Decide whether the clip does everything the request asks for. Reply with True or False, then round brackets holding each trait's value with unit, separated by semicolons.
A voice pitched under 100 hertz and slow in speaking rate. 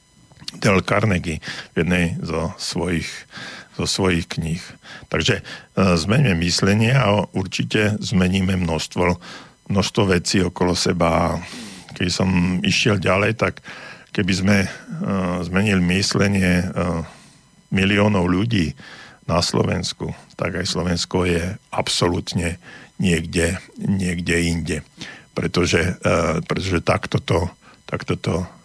True (90 Hz; 95 wpm)